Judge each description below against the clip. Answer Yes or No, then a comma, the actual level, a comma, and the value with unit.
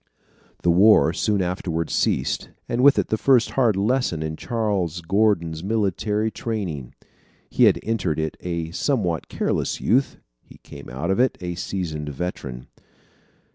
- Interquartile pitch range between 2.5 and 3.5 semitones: No, average, 5.1 semitones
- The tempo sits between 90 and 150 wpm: Yes, average, 145 wpm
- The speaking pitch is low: Yes, very low, 95 Hz